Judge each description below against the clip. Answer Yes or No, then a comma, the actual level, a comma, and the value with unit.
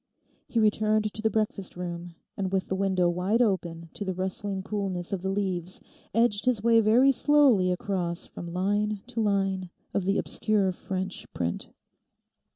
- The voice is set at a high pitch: Yes, high, 195 Hz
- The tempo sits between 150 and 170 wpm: Yes, average, 160 wpm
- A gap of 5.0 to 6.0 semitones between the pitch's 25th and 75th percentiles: No, average, 2.7 semitones